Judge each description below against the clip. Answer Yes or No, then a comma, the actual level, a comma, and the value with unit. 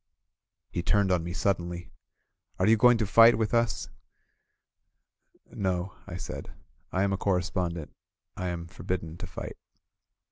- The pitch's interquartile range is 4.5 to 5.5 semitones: No, average, 2.8 semitones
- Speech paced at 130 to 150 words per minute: Yes, average, 145 wpm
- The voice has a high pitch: No, very low, 95 Hz